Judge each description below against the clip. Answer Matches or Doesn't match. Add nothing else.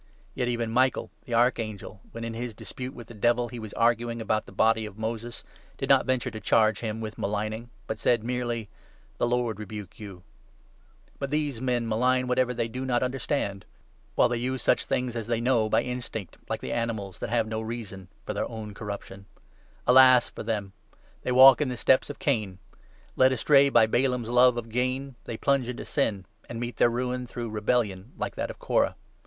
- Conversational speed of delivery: Doesn't match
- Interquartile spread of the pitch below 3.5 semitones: Matches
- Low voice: Matches